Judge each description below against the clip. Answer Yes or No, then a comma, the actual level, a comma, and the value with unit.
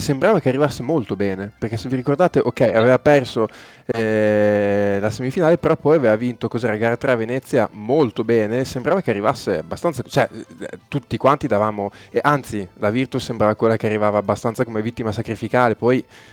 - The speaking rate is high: Yes, fast, 175 wpm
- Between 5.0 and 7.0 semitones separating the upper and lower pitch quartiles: No, average, 3.5 semitones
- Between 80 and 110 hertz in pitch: No, low, 120 Hz